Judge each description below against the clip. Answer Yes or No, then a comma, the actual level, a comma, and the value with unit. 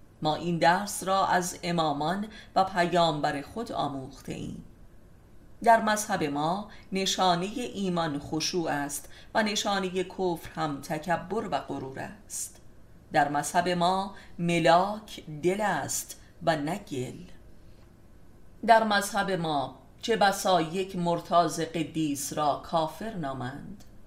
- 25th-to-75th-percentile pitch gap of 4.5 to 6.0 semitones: Yes, average, 5.0 semitones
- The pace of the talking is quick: No, average, 115 wpm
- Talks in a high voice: No, medium, 170 Hz